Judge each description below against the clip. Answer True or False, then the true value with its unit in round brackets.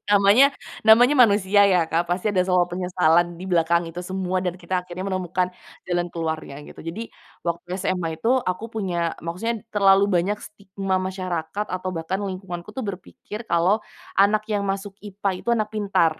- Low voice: False (185 Hz)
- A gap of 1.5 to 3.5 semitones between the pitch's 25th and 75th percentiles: True (2.6 semitones)